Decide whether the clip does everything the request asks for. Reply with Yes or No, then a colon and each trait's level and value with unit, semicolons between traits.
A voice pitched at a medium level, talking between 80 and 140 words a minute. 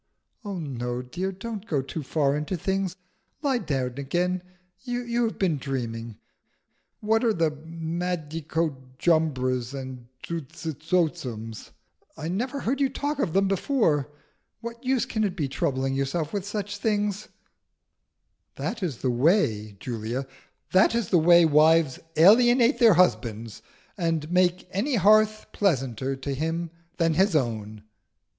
Yes: medium, 165 Hz; slow, 135 wpm